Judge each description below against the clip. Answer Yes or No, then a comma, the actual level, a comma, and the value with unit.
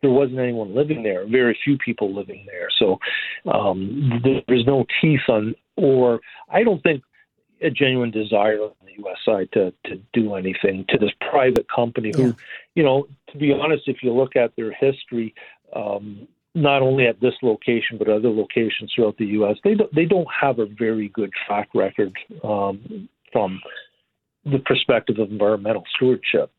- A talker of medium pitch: No, low, 120 Hz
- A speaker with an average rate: Yes, average, 170 wpm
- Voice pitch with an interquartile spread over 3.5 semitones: Yes, average, 4.4 semitones